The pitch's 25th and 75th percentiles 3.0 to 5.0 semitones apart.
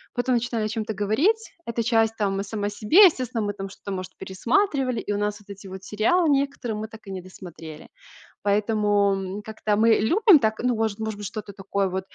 No: narrow, 2.6 semitones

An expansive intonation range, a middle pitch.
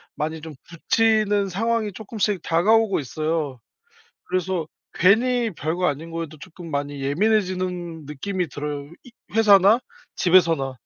No: average, 4.8 semitones; medium, 180 Hz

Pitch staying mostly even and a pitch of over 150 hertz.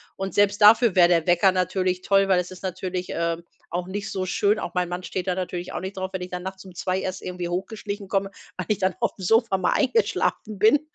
Yes: narrow, 1.7 semitones; medium, 185 Hz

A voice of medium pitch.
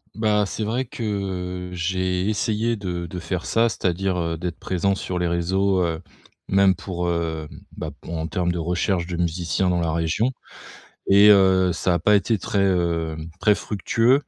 No: very low, 90 Hz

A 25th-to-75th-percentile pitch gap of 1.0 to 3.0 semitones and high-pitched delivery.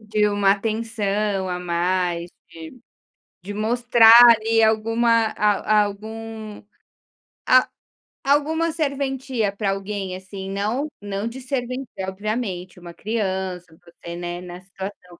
No: average, 3.4 semitones; high, 210 Hz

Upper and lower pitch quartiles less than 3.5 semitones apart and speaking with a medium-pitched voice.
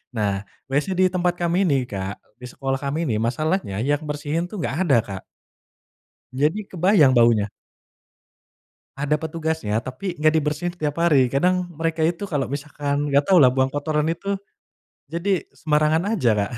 No: average, 4.2 semitones; medium, 150 Hz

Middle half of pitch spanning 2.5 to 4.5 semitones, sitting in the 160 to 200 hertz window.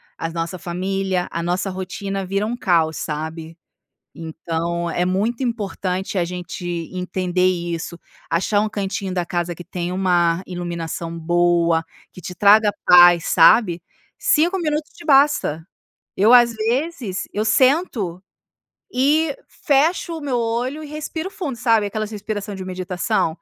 No: average, 5.2 semitones; high, 190 Hz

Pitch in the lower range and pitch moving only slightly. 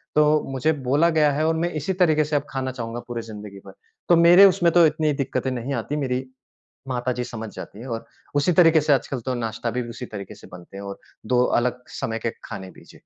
No: low, 130 Hz; average, 4.8 semitones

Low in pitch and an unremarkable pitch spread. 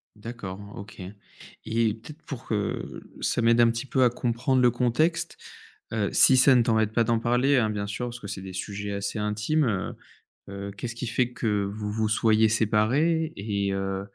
Yes: low, 110 Hz; average, 3.1 semitones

